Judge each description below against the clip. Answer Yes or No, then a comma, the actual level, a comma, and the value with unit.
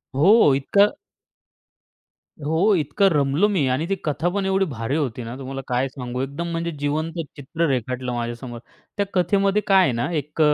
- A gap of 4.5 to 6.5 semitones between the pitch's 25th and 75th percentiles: Yes, average, 4.9 semitones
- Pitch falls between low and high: Yes, medium, 145 Hz